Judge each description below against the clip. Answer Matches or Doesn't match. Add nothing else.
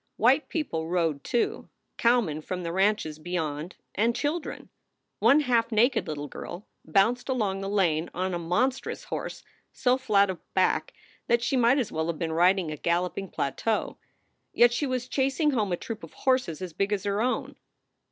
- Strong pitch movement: Matches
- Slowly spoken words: Doesn't match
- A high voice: Matches